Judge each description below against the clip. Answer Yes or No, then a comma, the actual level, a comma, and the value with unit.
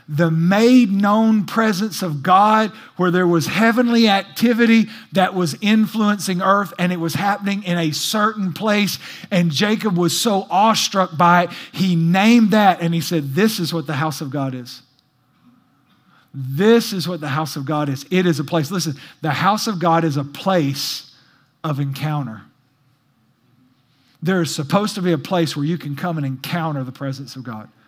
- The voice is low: No, medium, 175 Hz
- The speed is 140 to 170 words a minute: No, average, 180 wpm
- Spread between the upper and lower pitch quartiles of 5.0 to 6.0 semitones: Yes, wide, 5.6 semitones